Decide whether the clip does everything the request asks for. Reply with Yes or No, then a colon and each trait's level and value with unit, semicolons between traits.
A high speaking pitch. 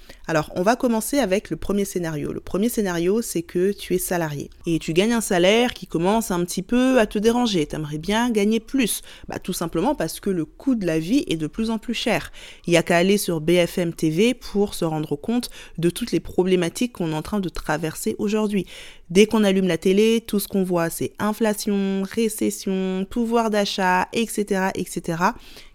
Yes: high, 195 Hz